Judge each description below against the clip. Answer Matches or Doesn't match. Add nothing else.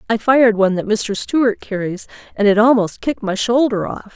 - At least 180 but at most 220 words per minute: Matches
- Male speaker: Doesn't match